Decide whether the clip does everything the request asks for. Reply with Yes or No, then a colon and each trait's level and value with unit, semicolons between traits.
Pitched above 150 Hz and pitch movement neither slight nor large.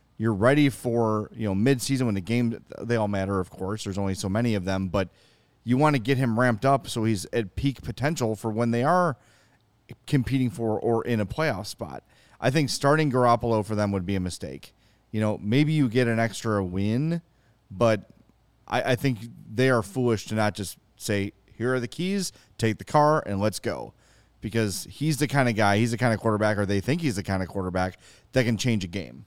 No: low, 115 Hz; average, 4.0 semitones